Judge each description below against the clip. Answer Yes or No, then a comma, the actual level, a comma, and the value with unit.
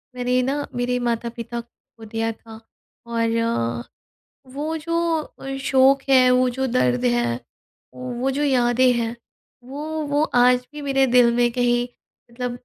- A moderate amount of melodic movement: No, narrow, 2.3 semitones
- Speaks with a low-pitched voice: No, high, 245 Hz